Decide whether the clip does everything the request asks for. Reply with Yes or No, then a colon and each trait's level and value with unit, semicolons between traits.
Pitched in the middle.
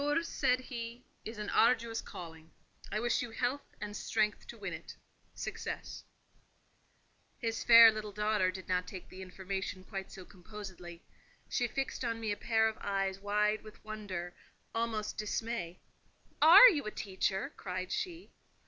No: high, 210 Hz